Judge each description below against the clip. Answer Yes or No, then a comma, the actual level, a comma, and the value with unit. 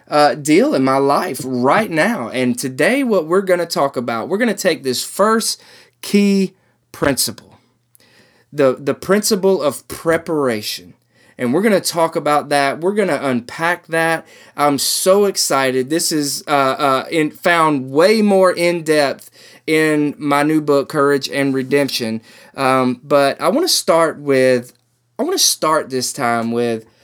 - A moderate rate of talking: Yes, average, 165 wpm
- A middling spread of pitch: Yes, average, 5.0 semitones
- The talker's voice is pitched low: No, medium, 145 Hz